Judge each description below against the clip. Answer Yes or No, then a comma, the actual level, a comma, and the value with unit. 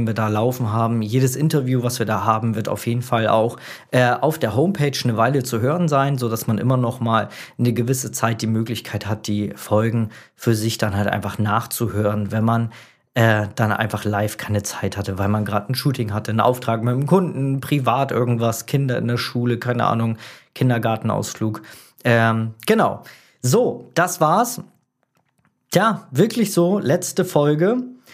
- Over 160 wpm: Yes, average, 175 wpm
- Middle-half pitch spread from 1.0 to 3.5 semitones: Yes, average, 2.9 semitones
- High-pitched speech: No, low, 115 Hz